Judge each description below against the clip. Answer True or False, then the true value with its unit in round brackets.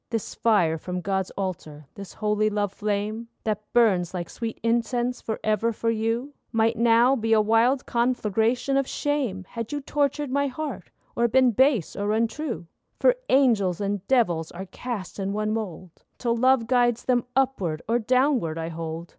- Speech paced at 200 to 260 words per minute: False (165 wpm)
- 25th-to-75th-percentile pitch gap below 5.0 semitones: True (4.0 semitones)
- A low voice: False (225 Hz)